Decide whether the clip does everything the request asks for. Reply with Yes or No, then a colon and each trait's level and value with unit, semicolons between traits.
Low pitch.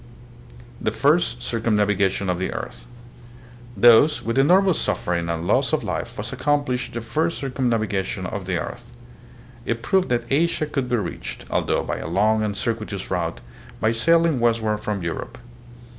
Yes: low, 115 Hz